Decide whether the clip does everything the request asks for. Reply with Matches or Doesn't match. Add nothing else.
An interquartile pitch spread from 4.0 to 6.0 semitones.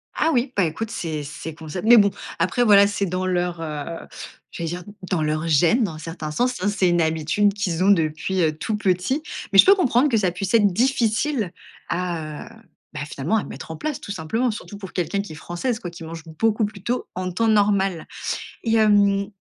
Matches